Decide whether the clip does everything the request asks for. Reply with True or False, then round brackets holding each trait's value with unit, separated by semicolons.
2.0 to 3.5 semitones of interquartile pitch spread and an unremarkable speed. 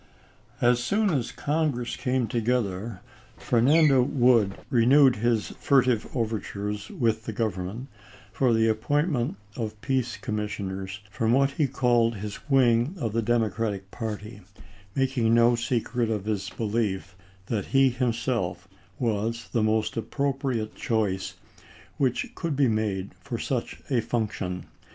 False (3.2 semitones; 130 wpm)